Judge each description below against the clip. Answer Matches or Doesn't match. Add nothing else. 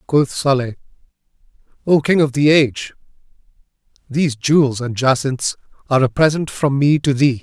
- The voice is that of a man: Matches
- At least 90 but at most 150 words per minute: Matches